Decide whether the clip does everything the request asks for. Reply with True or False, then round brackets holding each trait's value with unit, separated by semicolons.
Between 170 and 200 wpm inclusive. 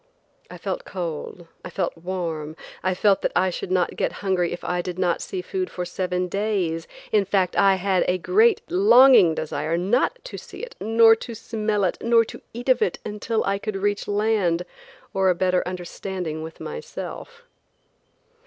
True (180 wpm)